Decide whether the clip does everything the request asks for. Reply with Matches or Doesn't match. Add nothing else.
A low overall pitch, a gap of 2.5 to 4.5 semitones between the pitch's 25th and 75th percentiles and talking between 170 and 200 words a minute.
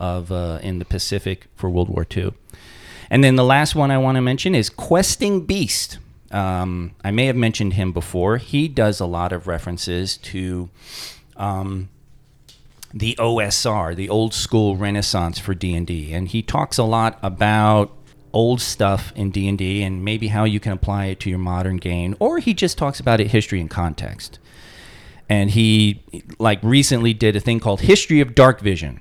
Matches